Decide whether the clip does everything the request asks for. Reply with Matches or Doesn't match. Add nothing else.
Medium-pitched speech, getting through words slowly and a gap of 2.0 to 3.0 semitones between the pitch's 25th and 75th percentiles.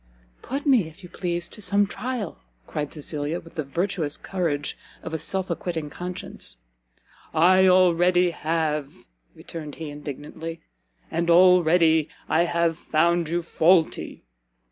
Matches